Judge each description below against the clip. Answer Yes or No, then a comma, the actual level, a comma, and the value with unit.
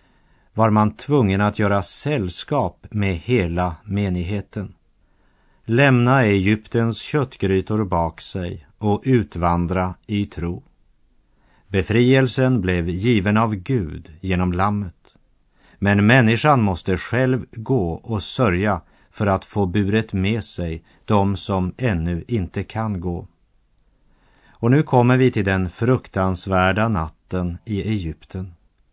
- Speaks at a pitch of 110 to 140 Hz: No, low, 100 Hz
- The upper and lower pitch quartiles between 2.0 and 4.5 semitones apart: Yes, average, 3.9 semitones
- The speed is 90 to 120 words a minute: Yes, slow, 110 wpm